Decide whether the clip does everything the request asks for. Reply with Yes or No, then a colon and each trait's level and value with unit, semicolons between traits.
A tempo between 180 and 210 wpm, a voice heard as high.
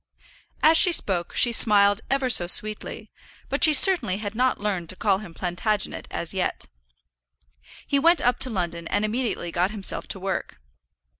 No: average, 165 wpm; high, 210 Hz